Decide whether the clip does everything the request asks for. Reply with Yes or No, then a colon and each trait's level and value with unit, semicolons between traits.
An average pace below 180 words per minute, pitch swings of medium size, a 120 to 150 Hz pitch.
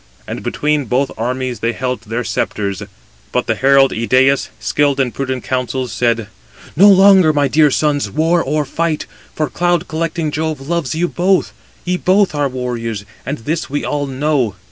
Yes: average, 165 wpm; average, 3.8 semitones; medium, 140 Hz